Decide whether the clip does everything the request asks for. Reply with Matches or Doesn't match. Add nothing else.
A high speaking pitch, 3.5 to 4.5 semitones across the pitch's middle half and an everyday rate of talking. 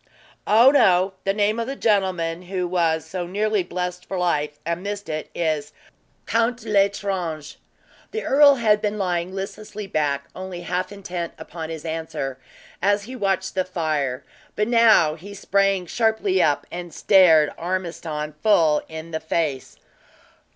Doesn't match